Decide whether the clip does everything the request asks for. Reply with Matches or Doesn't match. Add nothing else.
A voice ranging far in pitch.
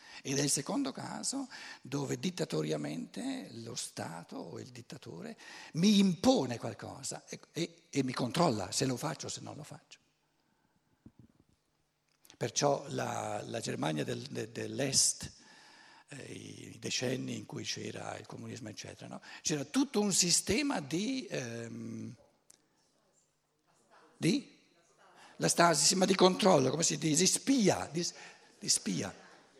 Matches